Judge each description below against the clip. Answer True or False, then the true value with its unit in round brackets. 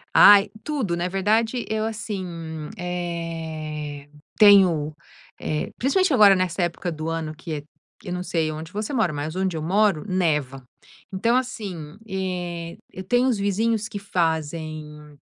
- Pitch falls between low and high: True (180 Hz)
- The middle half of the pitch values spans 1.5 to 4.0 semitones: False (4.5 semitones)